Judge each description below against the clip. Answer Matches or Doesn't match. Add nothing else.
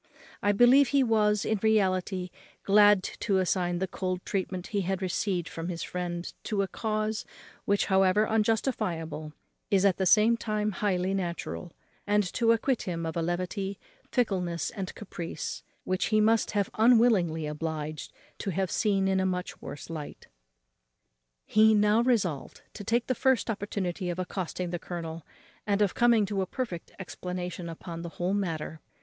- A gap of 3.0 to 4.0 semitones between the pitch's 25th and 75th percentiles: Matches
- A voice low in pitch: Doesn't match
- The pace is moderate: Matches